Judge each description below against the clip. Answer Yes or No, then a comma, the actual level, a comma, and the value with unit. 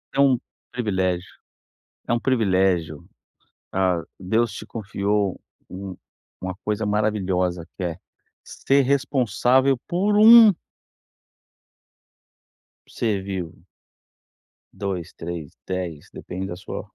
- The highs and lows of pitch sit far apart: No, average, 4.6 semitones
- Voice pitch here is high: No, low, 100 Hz